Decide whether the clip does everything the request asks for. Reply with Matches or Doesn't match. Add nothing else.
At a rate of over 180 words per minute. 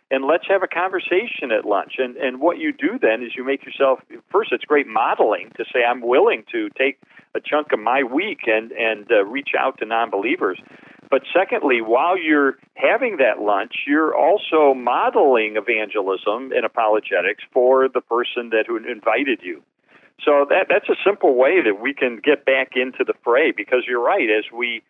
Matches